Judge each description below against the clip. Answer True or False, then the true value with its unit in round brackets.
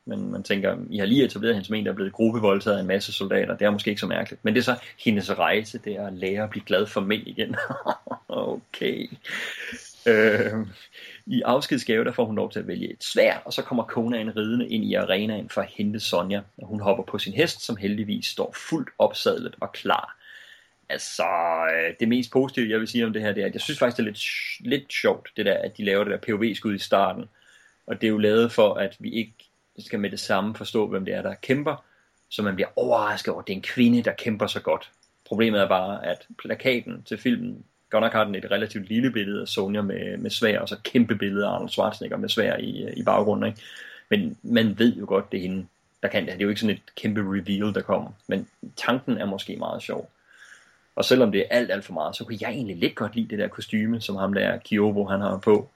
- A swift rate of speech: True (245 wpm)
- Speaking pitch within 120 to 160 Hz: False (105 Hz)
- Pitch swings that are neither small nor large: False (2.3 semitones)